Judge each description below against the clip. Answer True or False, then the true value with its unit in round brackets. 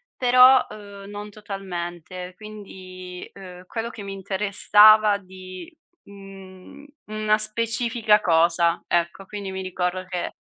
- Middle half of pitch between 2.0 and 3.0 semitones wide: True (2.5 semitones)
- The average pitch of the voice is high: True (195 Hz)